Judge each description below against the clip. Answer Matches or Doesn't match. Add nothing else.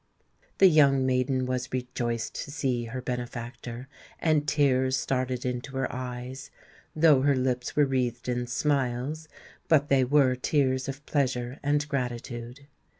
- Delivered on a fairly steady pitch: Matches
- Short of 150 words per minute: Matches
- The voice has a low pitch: Matches